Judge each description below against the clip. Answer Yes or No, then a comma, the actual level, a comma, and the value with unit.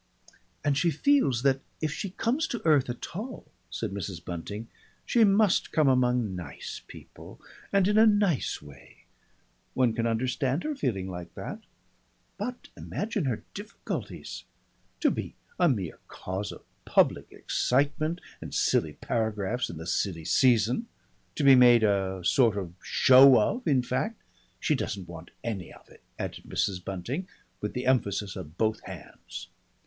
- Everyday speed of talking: Yes, average, 155 wpm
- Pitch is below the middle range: Yes, low, 125 Hz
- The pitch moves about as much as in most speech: No, wide, 8.4 semitones